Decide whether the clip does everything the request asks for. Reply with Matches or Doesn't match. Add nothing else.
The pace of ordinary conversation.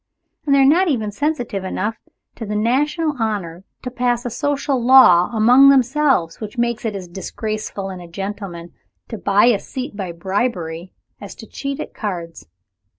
Matches